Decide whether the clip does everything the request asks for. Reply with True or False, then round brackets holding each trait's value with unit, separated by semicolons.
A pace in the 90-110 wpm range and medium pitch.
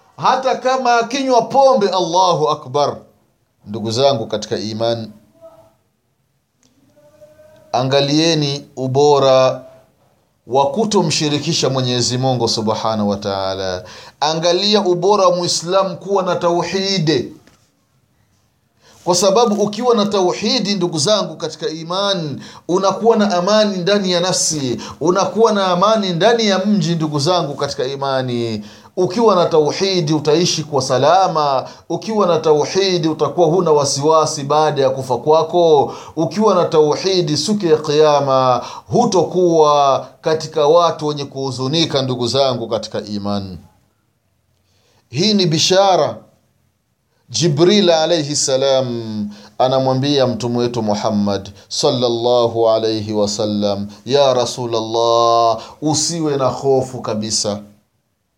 True (100 wpm; 150 Hz)